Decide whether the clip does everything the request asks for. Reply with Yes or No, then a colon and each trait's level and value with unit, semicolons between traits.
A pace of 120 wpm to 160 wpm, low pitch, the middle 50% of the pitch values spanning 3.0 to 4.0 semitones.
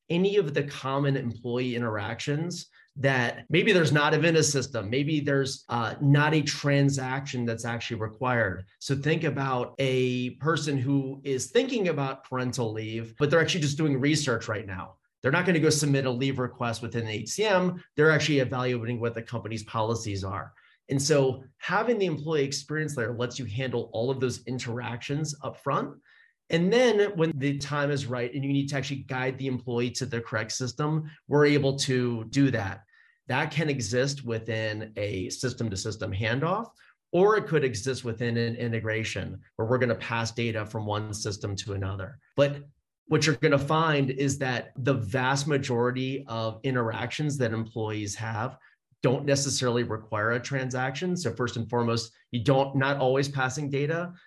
No: average, 175 wpm; low, 130 Hz; average, 3.6 semitones